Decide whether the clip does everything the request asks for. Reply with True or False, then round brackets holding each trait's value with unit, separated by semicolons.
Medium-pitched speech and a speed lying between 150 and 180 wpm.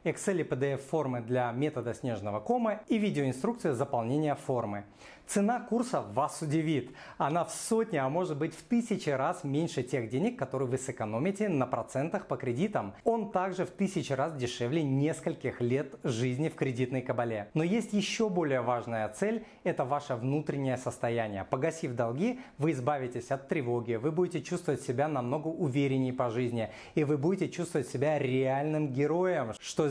True (145 Hz; 160 wpm)